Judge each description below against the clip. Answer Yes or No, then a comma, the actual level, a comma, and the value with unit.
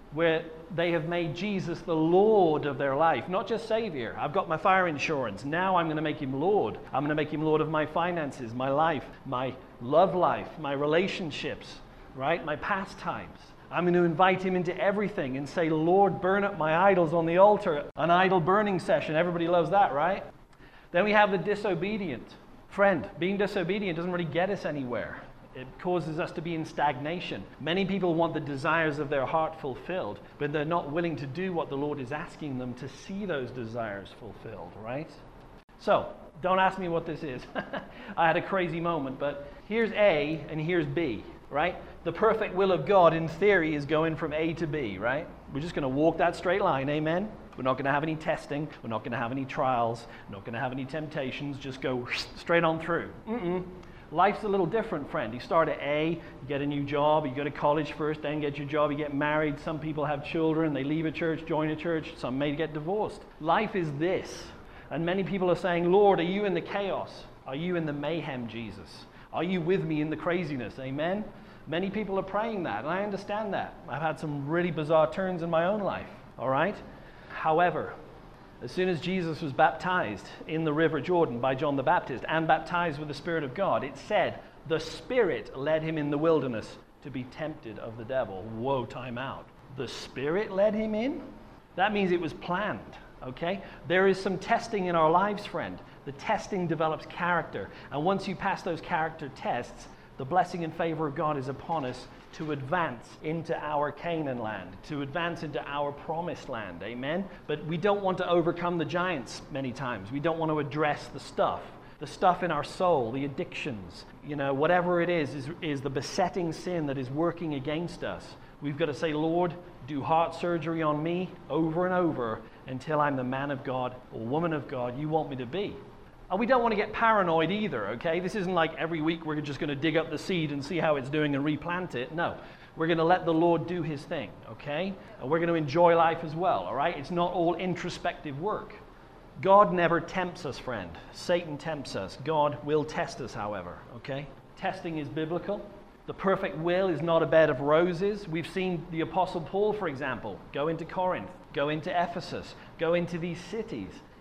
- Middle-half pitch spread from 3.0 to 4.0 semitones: Yes, average, 3.5 semitones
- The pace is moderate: No, fast, 210 wpm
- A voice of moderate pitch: Yes, medium, 165 Hz